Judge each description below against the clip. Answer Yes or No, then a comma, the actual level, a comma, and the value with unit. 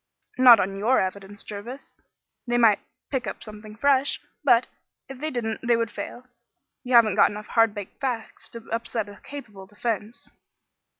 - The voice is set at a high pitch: Yes, high, 230 Hz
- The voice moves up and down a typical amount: Yes, average, 3.0 semitones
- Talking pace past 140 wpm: Yes, average, 165 wpm